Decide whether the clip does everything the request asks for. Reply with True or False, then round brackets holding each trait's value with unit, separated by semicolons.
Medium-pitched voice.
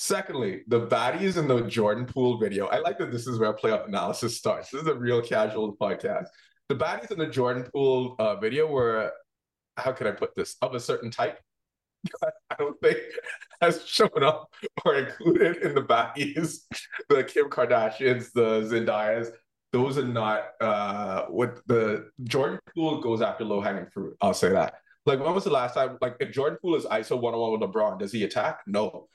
False (130 Hz)